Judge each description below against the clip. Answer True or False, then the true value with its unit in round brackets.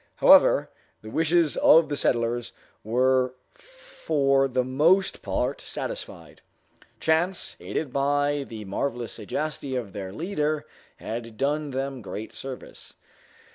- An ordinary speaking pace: False (115 wpm)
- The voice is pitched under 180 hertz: True (140 Hz)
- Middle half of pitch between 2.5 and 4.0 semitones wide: False (4.4 semitones)